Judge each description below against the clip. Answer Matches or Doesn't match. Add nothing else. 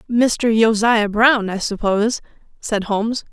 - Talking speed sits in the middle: Doesn't match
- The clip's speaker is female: Matches